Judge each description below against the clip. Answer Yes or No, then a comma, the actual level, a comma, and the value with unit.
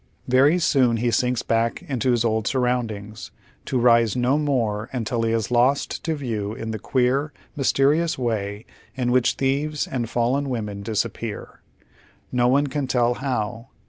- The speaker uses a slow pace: No, average, 155 wpm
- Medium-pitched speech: No, low, 125 Hz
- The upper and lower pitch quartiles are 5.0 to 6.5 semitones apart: No, average, 2.9 semitones